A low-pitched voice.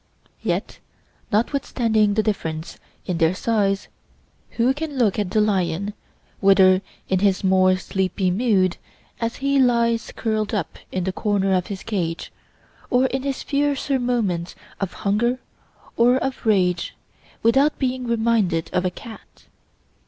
No: high, 210 Hz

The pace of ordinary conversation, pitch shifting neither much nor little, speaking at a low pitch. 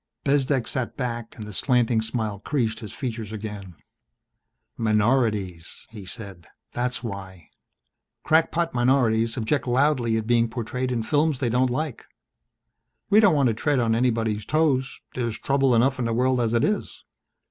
Yes: average, 155 wpm; average, 3.0 semitones; low, 120 Hz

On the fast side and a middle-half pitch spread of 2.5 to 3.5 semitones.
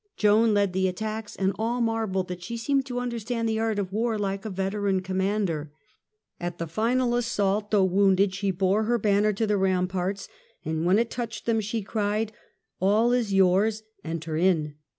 No: average, 185 wpm; average, 2.9 semitones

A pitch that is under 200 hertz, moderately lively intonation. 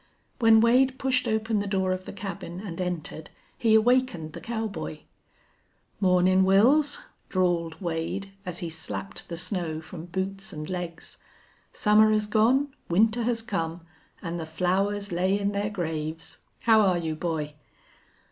Yes: high, 190 Hz; average, 4.5 semitones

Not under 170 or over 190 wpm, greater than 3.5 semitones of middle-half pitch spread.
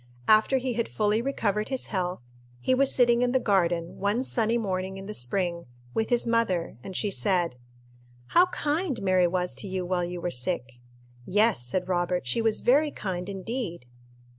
Yes: average, 180 wpm; average, 4.8 semitones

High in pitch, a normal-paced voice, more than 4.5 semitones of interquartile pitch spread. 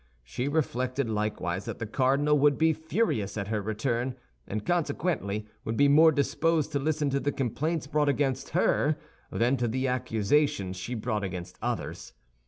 No: low, 130 Hz; average, 165 wpm; wide, 5.5 semitones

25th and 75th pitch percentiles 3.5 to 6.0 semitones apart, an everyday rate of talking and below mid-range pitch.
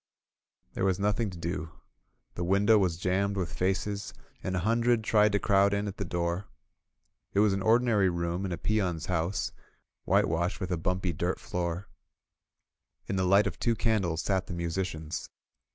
No: average, 2.7 semitones; average, 170 wpm; very low, 95 Hz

